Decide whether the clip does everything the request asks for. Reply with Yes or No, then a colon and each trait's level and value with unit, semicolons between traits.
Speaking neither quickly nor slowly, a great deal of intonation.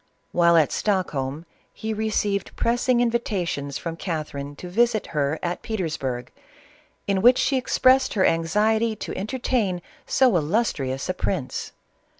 No: slow, 130 wpm; wide, 6.2 semitones